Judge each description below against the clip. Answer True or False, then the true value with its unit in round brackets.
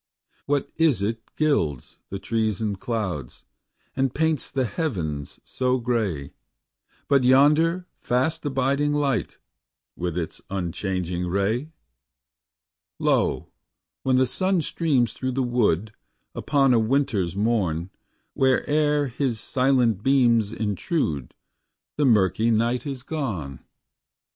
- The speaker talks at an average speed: False (110 wpm)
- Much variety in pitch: True (5.9 semitones)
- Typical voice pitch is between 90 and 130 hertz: True (120 Hz)